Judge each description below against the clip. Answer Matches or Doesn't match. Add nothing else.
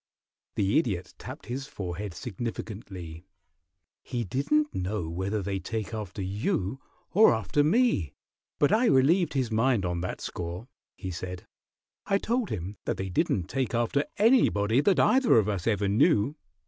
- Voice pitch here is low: Matches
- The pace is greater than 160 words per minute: Doesn't match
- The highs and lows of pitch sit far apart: Matches